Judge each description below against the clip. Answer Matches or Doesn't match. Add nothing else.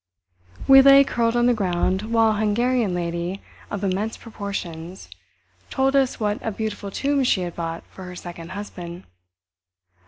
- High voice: Matches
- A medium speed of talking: Matches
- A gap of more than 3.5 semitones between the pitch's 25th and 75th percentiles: Matches